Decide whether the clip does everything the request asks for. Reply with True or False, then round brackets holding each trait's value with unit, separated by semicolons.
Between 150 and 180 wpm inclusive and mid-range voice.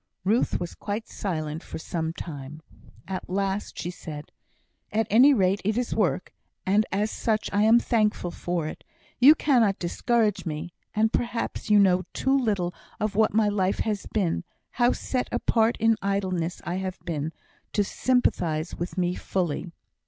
False (160 wpm; 195 Hz)